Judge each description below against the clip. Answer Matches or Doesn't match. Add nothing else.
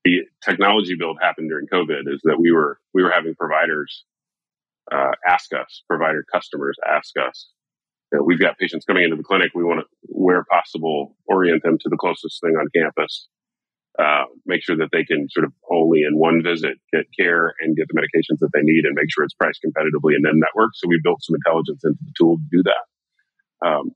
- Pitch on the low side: Matches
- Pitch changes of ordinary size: Doesn't match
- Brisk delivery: Matches